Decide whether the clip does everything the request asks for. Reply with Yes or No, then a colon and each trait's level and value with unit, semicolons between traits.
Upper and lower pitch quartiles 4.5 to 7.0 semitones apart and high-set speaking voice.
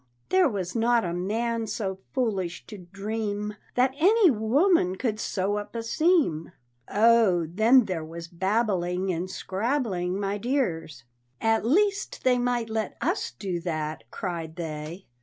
Yes: average, 5.1 semitones; high, 205 Hz